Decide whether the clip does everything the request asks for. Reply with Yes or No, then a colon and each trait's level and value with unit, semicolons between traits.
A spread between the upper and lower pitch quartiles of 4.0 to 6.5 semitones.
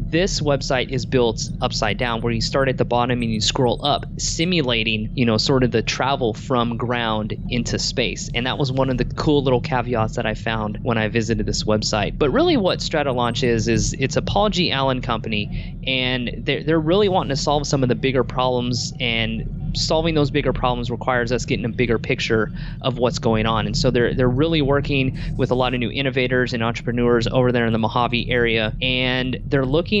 No: average, 3.2 semitones